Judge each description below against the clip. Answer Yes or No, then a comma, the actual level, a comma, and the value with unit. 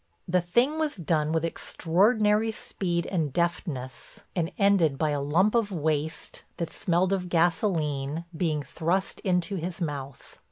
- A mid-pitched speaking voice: Yes, medium, 170 Hz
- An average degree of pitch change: Yes, average, 3.8 semitones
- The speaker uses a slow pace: No, average, 145 wpm